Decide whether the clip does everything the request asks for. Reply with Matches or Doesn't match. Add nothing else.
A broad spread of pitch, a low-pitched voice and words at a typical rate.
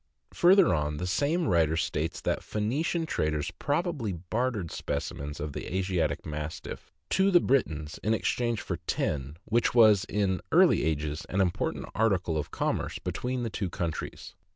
Matches